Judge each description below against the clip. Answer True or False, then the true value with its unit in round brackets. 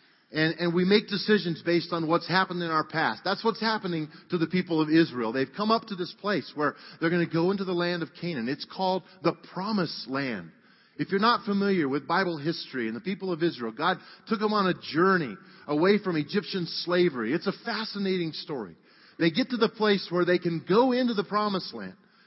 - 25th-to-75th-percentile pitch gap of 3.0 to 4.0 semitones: True (3.5 semitones)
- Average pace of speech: False (215 wpm)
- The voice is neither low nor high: True (180 Hz)